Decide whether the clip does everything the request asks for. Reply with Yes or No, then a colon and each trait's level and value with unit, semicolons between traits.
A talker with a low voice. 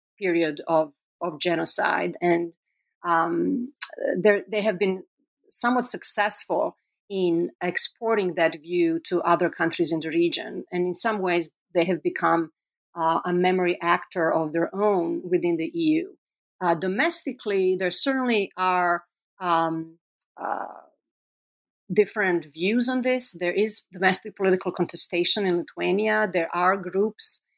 No: medium, 185 Hz